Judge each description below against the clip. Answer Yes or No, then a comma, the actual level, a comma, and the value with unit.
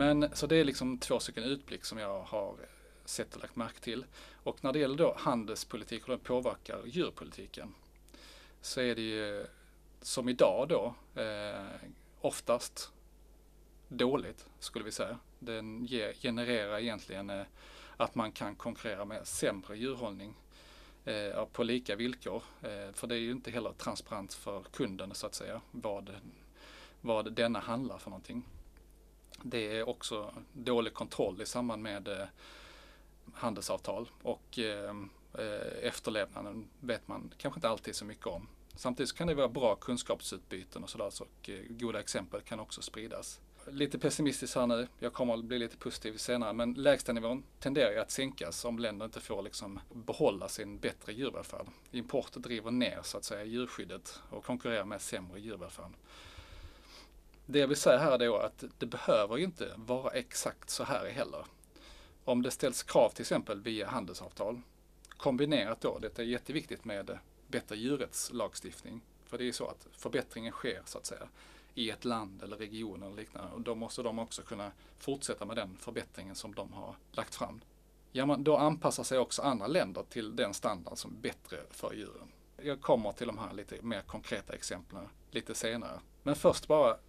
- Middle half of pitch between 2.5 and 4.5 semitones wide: Yes, average, 2.8 semitones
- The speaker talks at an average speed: Yes, average, 165 wpm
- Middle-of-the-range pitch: No, low, 115 Hz